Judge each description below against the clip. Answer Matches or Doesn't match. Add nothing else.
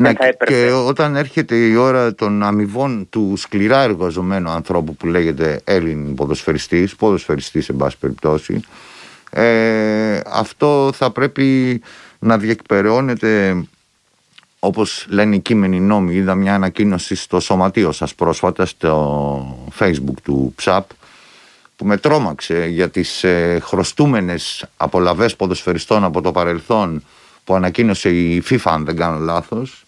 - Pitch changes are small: Doesn't match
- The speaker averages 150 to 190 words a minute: Doesn't match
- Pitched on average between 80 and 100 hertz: Matches